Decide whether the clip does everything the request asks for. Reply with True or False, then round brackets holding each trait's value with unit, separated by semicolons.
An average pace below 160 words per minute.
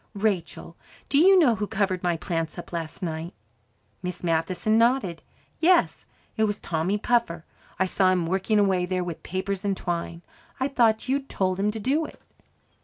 False (175 wpm)